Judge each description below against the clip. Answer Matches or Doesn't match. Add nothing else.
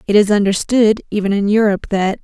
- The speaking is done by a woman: Matches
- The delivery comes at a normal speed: Matches